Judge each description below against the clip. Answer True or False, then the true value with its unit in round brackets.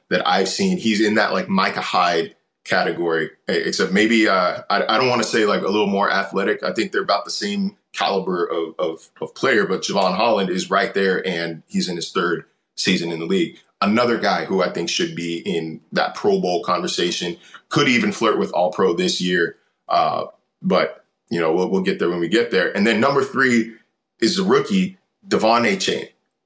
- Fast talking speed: True (210 wpm)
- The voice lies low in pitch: True (110 Hz)